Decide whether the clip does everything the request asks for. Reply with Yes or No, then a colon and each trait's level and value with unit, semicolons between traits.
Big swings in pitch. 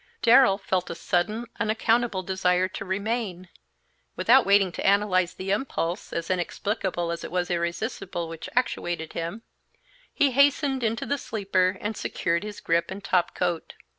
No: average, 3.9 semitones